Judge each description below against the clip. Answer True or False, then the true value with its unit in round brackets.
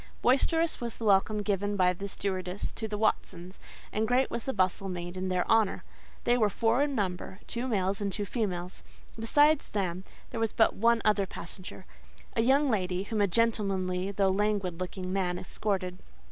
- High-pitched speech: True (200 Hz)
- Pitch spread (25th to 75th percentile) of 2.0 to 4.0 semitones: True (3.4 semitones)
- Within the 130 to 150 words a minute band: False (175 wpm)